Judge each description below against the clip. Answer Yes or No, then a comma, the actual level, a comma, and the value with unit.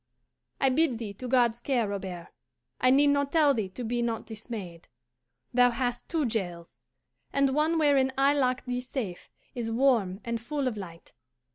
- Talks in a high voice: Yes, high, 245 Hz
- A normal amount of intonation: Yes, average, 3.9 semitones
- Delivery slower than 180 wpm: Yes, average, 170 wpm